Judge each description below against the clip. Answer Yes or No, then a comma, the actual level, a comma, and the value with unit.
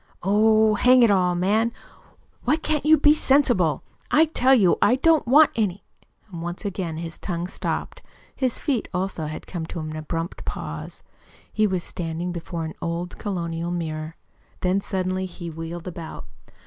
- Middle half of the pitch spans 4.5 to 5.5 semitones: Yes, average, 5.2 semitones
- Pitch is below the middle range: No, medium, 185 Hz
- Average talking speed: Yes, average, 160 wpm